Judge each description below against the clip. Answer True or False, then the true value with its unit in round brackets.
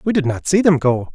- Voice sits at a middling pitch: True (150 Hz)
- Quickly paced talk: True (315 wpm)